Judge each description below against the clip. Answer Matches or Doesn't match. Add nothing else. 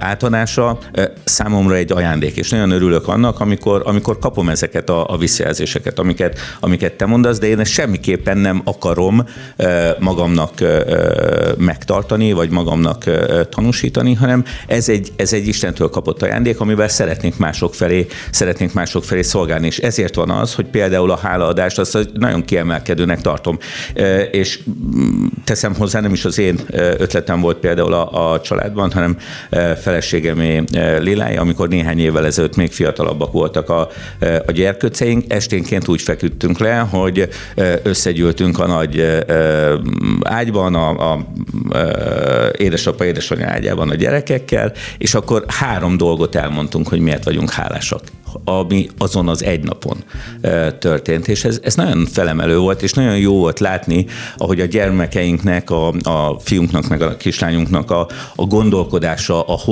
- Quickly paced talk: Doesn't match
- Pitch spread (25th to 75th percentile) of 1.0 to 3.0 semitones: Doesn't match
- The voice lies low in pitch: Matches